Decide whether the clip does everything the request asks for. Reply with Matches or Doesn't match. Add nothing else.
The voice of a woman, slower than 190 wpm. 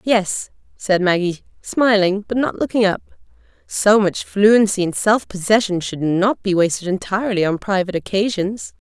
Matches